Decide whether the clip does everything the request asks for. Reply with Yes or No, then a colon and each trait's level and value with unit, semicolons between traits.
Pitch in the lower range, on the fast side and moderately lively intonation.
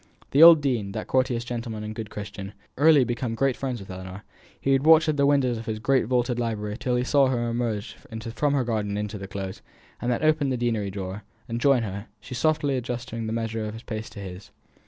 Yes: low, 115 Hz; fast, 230 wpm; average, 3.7 semitones